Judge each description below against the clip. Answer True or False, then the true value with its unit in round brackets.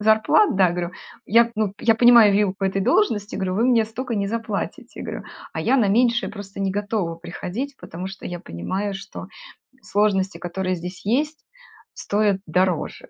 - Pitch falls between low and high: False (205 Hz)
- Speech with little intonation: False (3.2 semitones)